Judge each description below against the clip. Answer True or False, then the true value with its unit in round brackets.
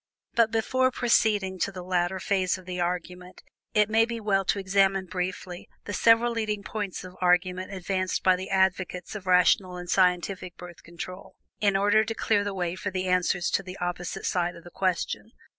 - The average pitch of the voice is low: False (185 Hz)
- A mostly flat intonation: True (2.2 semitones)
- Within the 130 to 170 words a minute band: False (190 wpm)